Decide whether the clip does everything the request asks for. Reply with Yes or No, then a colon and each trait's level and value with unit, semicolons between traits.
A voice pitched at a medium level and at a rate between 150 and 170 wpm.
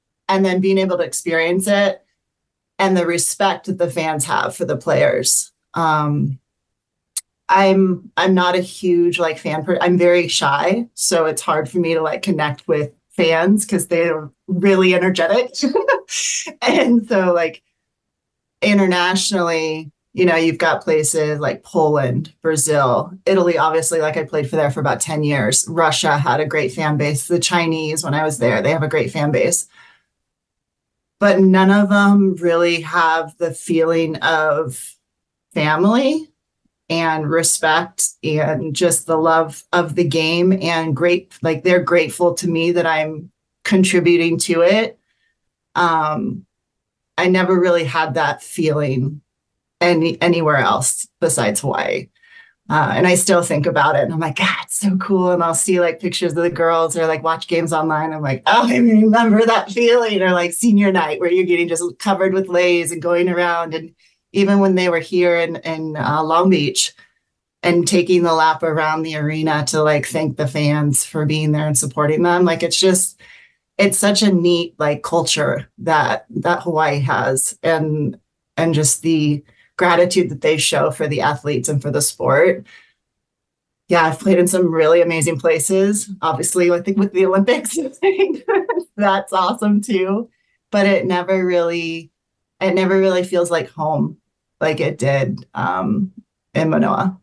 Yes: medium, 170 Hz; average, 165 wpm